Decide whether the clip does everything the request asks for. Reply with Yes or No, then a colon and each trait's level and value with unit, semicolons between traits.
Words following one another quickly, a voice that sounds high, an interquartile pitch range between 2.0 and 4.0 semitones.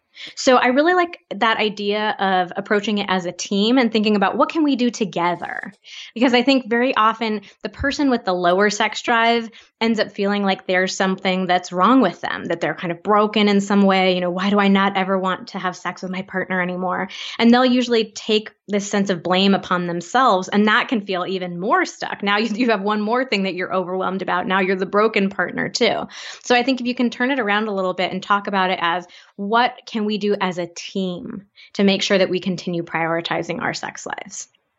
Yes: fast, 230 wpm; high, 205 Hz; average, 3.7 semitones